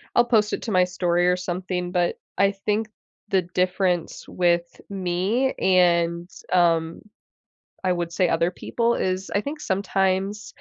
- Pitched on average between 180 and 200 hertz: Yes, medium, 185 Hz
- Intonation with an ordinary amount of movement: No, narrow, 2.1 semitones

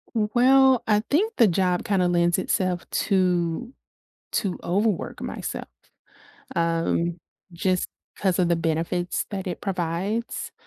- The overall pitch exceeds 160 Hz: Yes, medium, 185 Hz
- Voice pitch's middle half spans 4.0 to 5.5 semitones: No, average, 3.4 semitones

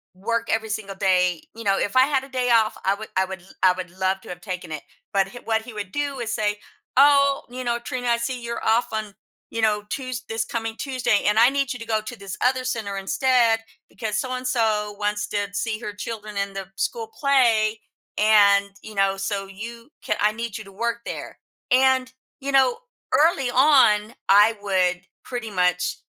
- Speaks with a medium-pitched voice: No, high, 220 Hz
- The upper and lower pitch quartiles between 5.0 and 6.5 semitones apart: No, average, 3.9 semitones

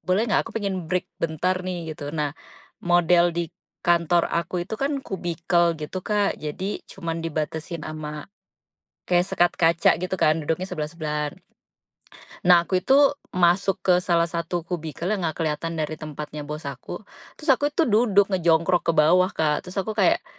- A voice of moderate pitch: Yes, medium, 170 Hz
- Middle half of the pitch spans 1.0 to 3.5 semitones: Yes, average, 2.7 semitones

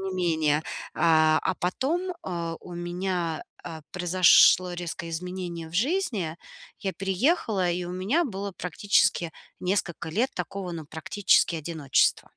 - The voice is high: No, medium, 180 Hz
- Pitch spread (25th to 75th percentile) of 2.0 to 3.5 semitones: Yes, narrow, 2.6 semitones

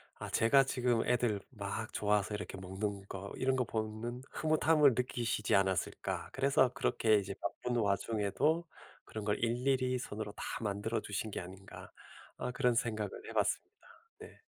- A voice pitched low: Yes, low, 110 Hz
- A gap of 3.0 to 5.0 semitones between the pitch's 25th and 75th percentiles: Yes, average, 3.5 semitones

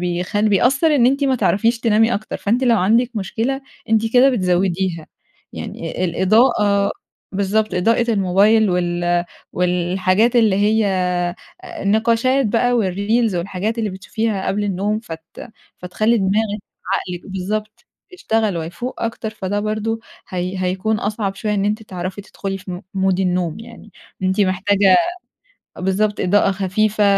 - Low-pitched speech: No, high, 205 Hz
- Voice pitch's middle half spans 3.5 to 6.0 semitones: No, average, 3.0 semitones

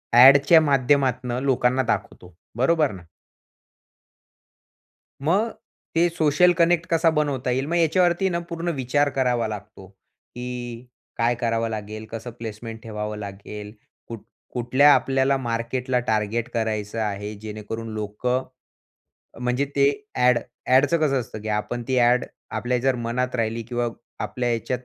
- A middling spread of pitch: Yes, average, 3.4 semitones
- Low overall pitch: Yes, low, 125 Hz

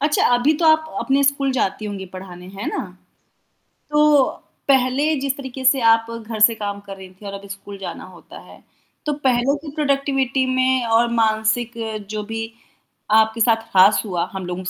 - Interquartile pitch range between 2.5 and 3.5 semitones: No, average, 5.0 semitones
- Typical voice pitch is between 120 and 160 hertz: No, high, 230 Hz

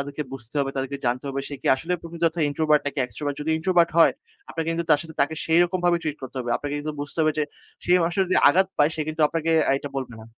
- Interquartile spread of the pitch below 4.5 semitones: Yes, average, 2.8 semitones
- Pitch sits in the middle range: Yes, medium, 155 Hz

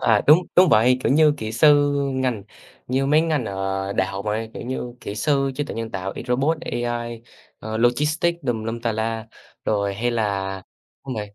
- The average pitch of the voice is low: Yes, low, 120 Hz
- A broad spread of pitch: No, average, 4.3 semitones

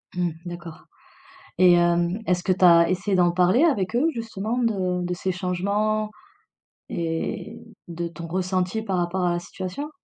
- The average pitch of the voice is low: No, medium, 180 Hz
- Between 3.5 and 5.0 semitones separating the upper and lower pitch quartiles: No, average, 2.9 semitones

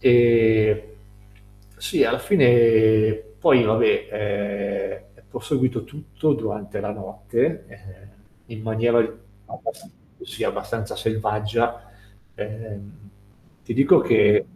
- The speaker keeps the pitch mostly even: Yes, narrow, 2.3 semitones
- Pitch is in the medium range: No, low, 110 Hz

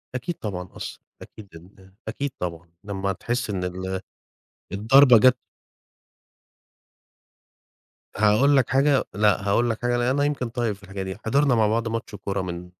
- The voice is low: Yes, low, 110 Hz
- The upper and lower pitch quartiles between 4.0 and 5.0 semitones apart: Yes, average, 4.5 semitones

